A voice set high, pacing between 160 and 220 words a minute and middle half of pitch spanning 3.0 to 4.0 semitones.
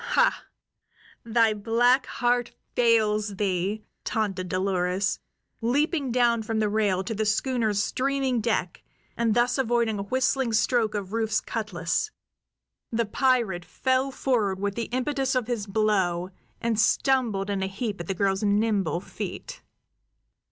No: high, 220 Hz; slow, 135 wpm; average, 3.4 semitones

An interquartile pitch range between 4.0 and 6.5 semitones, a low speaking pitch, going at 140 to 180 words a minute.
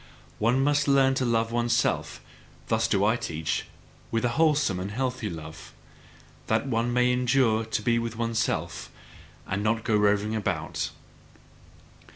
No: narrow, 2.6 semitones; low, 115 Hz; average, 145 wpm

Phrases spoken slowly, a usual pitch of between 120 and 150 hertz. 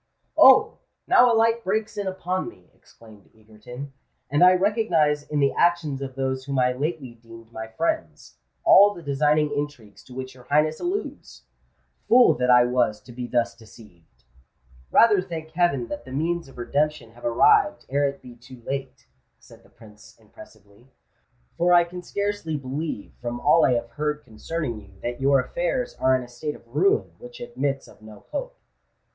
No: average, 175 wpm; medium, 140 Hz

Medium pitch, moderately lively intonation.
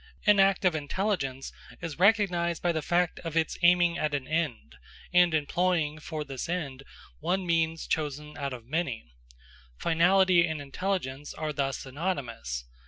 Yes: medium, 160 Hz; average, 4.0 semitones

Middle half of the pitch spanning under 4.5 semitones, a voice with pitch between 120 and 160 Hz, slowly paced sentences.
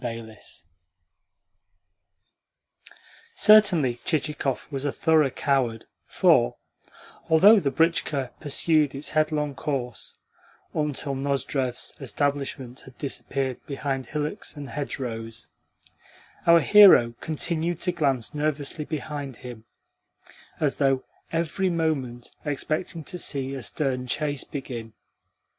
Yes: average, 3.0 semitones; medium, 140 Hz; slow, 105 wpm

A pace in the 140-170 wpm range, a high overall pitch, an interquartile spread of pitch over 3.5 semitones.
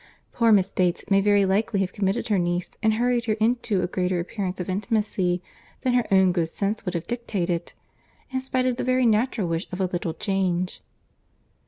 No: average, 195 wpm; high, 195 Hz; average, 4.0 semitones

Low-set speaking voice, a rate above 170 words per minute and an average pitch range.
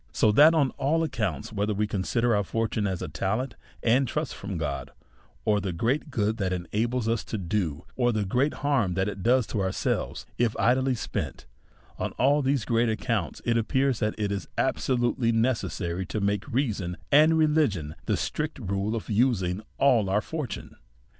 Yes: low, 110 Hz; average, 185 wpm; average, 4.6 semitones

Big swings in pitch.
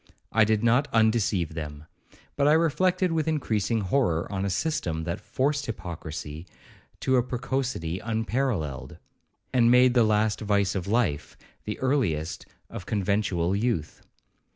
Yes: wide, 6.5 semitones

